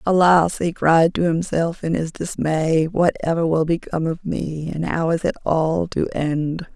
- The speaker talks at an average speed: Yes, average, 185 wpm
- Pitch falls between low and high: Yes, medium, 165 Hz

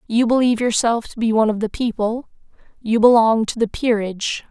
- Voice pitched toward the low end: No, high, 225 Hz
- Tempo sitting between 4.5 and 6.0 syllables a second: Yes, 5.8 syllables/s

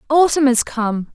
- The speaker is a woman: Yes, female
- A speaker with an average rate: Yes, average, 155 wpm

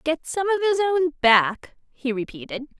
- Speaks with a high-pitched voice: Yes, very high, 295 Hz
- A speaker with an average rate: Yes, average, 170 wpm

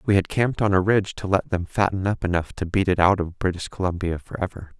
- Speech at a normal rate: No, fast, 265 wpm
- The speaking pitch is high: No, very low, 95 Hz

